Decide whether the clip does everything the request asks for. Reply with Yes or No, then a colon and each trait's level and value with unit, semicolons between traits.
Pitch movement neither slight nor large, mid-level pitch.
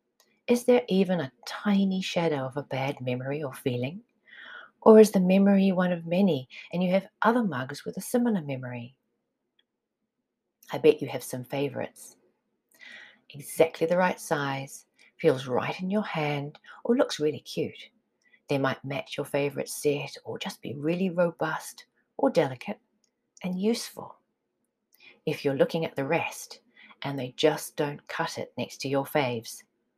No: wide, 5.7 semitones; medium, 165 Hz